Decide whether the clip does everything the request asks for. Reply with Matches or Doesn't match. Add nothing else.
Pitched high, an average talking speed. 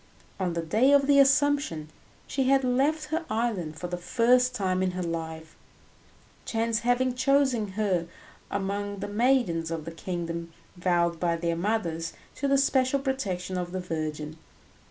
Matches